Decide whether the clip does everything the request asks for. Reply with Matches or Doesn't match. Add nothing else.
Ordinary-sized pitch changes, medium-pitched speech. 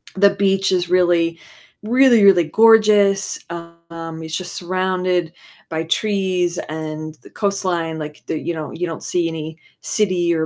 Matches